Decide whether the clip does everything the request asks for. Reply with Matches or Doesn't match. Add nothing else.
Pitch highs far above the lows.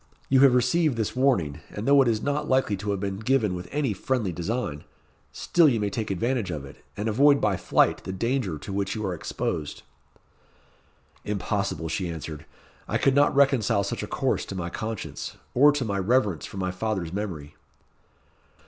Matches